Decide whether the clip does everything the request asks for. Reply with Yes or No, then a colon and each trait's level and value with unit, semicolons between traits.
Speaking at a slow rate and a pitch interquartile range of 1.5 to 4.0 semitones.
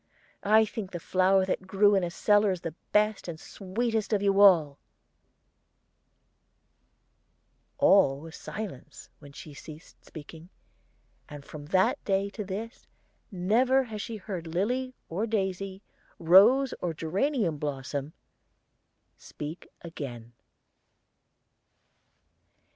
No: slow, 110 wpm; average, 4.7 semitones